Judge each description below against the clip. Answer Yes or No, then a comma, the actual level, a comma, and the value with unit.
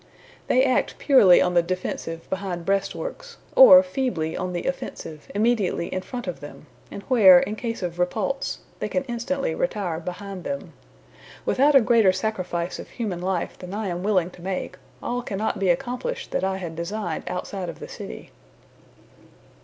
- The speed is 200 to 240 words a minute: No, average, 170 wpm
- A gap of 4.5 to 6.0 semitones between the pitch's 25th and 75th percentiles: Yes, average, 5.3 semitones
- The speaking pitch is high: Yes, high, 195 Hz